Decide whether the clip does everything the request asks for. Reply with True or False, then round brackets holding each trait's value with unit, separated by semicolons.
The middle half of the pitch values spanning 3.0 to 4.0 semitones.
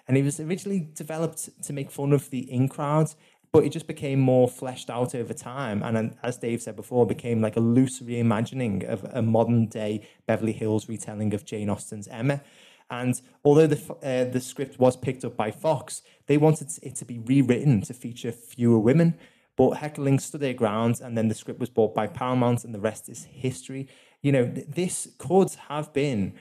True (3.7 semitones)